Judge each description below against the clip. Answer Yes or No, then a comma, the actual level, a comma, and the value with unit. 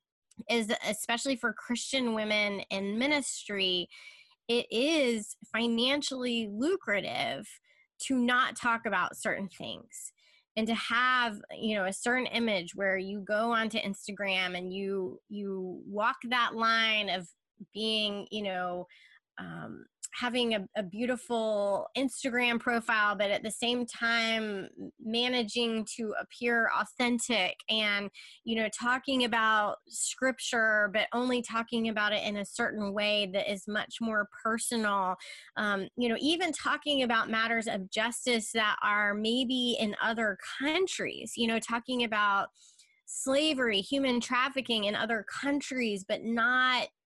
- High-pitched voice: Yes, high, 225 Hz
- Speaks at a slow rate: Yes, slow, 130 wpm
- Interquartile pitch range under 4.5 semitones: Yes, average, 3.1 semitones